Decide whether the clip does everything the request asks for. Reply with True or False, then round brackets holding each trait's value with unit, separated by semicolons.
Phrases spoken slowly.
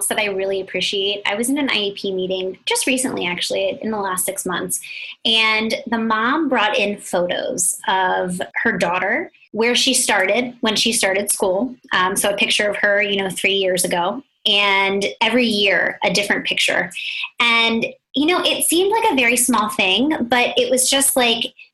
False (180 wpm)